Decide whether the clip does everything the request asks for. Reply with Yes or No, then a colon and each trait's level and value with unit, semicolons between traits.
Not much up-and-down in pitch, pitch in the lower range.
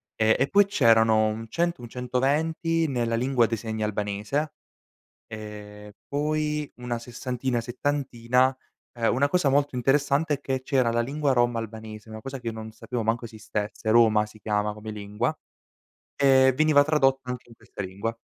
No: average, 4.0 semitones; low, 120 Hz